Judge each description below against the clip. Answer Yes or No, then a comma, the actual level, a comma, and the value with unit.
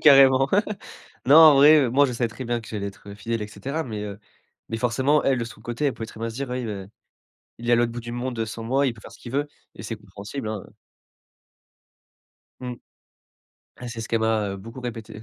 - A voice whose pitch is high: No, low, 120 Hz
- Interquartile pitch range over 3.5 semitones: No, average, 3.0 semitones